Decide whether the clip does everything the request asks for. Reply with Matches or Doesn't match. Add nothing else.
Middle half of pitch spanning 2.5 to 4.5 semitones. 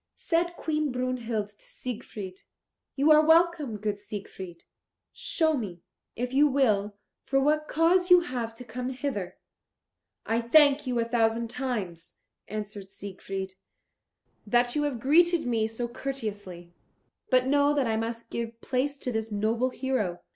Doesn't match